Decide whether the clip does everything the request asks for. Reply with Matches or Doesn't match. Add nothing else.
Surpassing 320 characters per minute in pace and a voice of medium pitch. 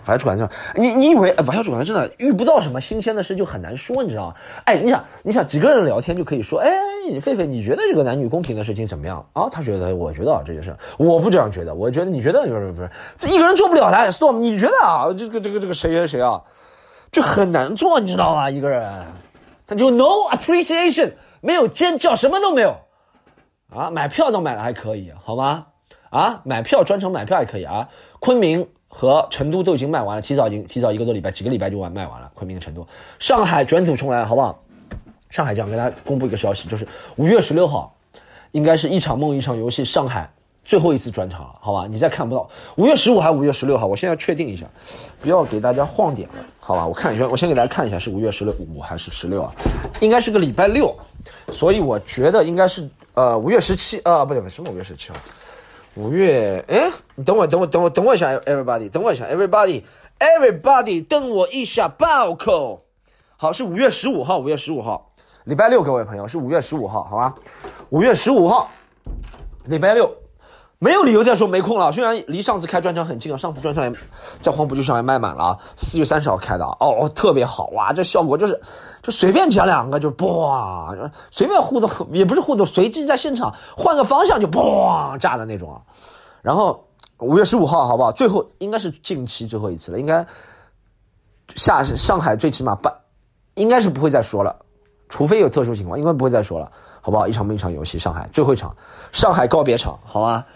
Matches